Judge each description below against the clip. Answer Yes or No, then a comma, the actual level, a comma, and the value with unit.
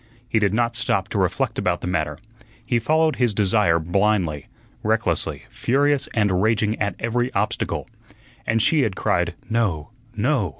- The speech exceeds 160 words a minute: No, average, 155 wpm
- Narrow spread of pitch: No, average, 4.3 semitones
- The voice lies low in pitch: Yes, low, 110 Hz